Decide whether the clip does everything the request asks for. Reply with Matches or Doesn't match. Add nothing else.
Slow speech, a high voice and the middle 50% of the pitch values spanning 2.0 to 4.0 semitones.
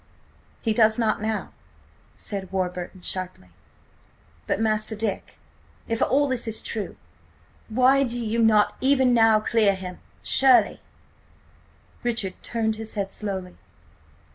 Matches